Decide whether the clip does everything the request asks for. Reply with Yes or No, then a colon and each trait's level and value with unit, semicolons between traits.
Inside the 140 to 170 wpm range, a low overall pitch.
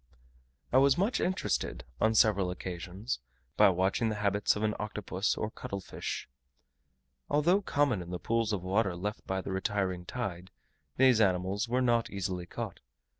Yes: average, 160 wpm; low, 105 Hz